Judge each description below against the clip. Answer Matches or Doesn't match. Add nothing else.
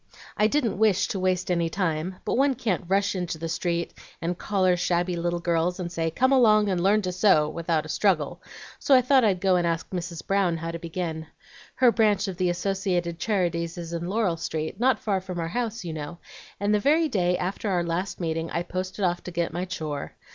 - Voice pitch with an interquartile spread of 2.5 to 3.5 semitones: Matches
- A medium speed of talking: Doesn't match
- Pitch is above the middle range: Doesn't match